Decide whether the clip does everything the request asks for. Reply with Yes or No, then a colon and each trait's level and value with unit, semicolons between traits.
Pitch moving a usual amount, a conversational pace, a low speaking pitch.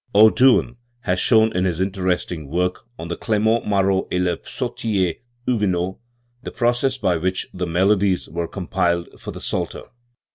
Yes: average, 3.7 semitones; average, 155 wpm; very low, 95 Hz